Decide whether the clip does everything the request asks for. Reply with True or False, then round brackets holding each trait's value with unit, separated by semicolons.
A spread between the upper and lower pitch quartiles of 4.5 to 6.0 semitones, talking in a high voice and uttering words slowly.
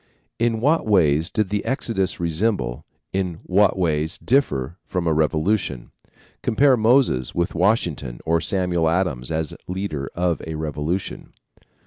False (4.9 semitones; 90 Hz; 130 wpm)